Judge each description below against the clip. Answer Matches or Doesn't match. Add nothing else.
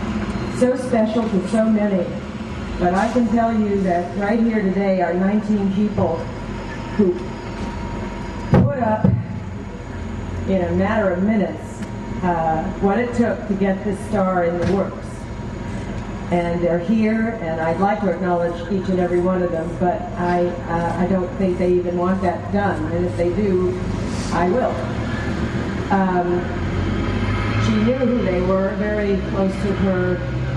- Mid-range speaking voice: Matches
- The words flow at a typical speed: Matches